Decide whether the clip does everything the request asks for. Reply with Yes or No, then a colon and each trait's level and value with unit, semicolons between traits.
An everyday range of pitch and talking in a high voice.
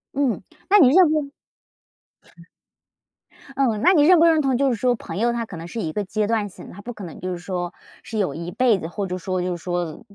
No: wide, 6.7 semitones; high, 215 Hz